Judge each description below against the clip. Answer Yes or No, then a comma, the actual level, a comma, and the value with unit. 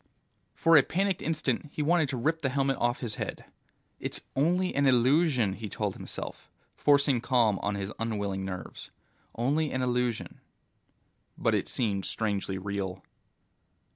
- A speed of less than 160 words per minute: Yes, average, 145 wpm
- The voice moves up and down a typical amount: No, wide, 6.0 semitones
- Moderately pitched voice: No, low, 125 Hz